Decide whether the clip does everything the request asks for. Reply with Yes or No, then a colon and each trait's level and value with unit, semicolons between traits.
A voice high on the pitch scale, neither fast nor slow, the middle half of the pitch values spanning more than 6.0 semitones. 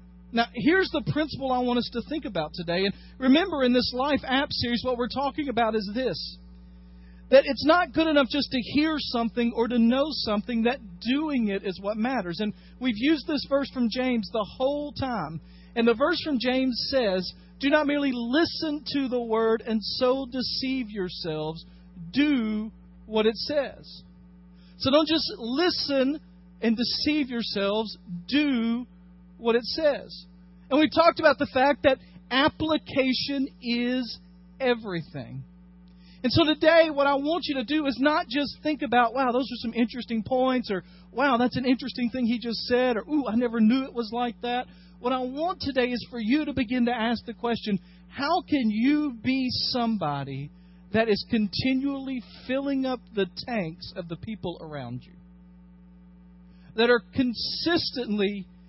Yes: high, 240 Hz; average, 170 wpm; wide, 6.5 semitones